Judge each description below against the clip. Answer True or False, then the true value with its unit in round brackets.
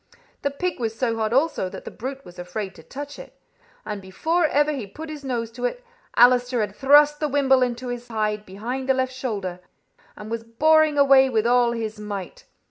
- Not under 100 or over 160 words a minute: False (205 wpm)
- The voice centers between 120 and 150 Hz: False (245 Hz)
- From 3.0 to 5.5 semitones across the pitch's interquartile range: True (4.4 semitones)